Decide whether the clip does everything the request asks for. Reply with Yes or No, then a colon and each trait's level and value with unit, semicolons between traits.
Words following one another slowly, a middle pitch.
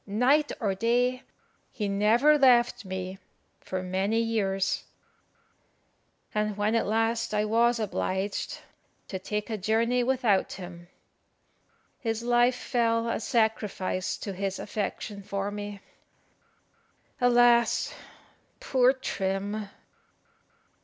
No: slow, 105 wpm; high, 220 Hz